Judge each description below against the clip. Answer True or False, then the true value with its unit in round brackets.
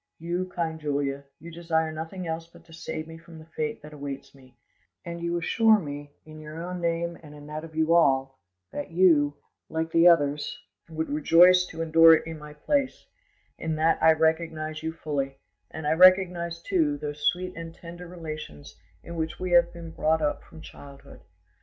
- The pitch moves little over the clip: True (2.1 semitones)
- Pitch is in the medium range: True (160 Hz)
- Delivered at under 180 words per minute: False (190 wpm)